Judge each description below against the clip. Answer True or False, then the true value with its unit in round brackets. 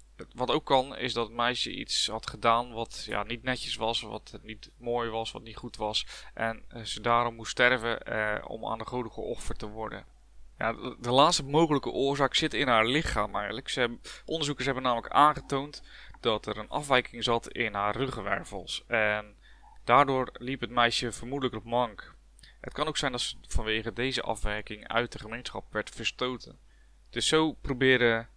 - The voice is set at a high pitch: False (120 Hz)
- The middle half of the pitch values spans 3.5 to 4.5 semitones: False (2.8 semitones)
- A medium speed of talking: True (180 wpm)